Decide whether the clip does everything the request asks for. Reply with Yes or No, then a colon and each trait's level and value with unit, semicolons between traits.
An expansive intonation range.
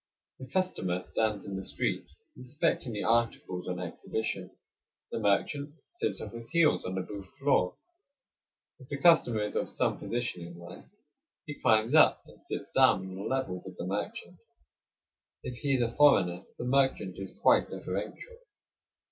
Yes: wide, 6.2 semitones